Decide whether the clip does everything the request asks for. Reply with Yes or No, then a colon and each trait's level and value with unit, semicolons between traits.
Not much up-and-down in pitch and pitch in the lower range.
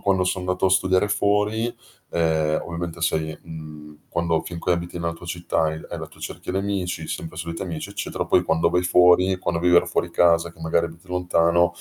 Yes: narrow, 1.7 semitones; very low, 85 Hz